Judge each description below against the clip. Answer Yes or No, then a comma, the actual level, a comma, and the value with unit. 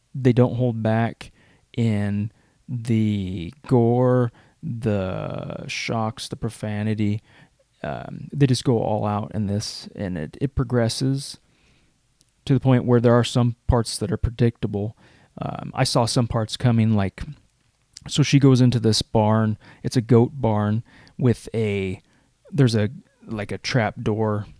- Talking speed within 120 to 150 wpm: Yes, average, 145 wpm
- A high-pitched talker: No, low, 115 Hz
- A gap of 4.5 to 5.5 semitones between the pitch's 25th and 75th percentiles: No, average, 3.2 semitones